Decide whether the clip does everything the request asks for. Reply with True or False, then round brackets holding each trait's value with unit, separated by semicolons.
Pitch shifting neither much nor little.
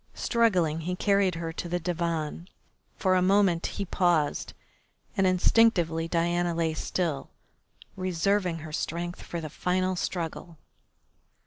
False (2.0 semitones)